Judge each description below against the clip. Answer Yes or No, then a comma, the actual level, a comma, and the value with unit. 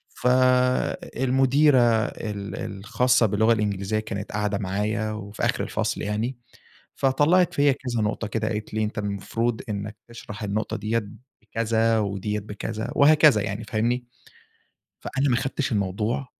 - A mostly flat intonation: No, average, 3.3 semitones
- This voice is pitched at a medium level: No, low, 110 Hz